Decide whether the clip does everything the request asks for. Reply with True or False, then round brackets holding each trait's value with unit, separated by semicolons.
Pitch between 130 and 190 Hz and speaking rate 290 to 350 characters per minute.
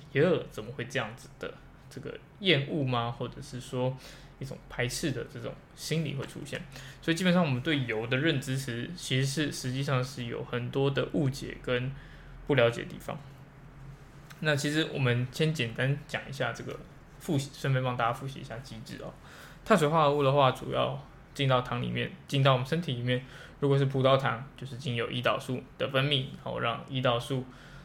True (135 Hz; 295 characters per minute)